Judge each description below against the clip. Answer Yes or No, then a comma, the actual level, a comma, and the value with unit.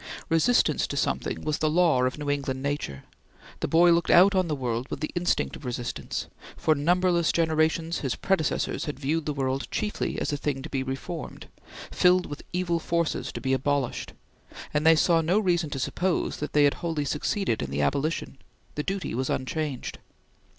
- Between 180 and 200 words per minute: Yes, average, 185 wpm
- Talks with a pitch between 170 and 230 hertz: No, medium, 155 Hz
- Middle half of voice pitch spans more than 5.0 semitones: No, average, 3.9 semitones